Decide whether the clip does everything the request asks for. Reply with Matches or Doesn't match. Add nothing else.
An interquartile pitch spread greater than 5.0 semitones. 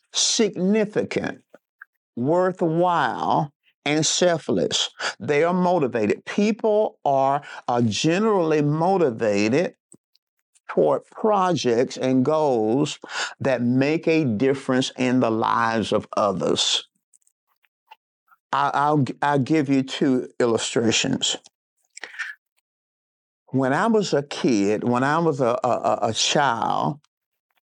Matches